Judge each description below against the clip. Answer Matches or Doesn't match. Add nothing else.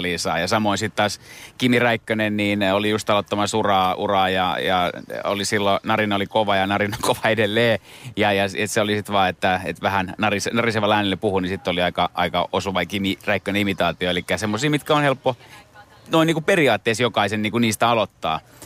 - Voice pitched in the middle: Doesn't match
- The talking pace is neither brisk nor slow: Doesn't match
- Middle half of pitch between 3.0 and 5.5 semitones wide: Doesn't match